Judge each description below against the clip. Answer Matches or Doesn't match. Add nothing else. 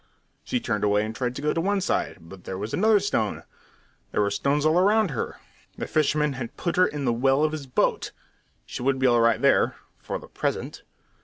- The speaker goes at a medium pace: Doesn't match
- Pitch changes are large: Matches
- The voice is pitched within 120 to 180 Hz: Matches